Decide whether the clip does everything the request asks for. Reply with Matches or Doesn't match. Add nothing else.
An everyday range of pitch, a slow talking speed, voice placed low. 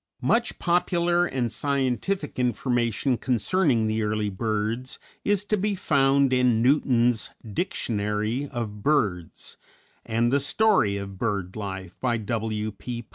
Matches